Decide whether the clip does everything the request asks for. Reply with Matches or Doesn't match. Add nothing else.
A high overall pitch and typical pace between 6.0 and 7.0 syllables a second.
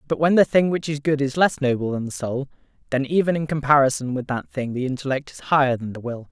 Doesn't match